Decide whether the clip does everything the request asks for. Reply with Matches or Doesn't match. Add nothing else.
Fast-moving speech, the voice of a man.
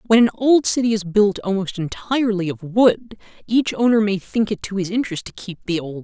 Matches